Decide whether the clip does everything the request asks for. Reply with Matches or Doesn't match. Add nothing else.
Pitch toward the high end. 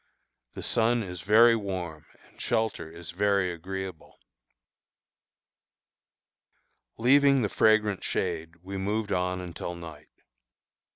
Doesn't match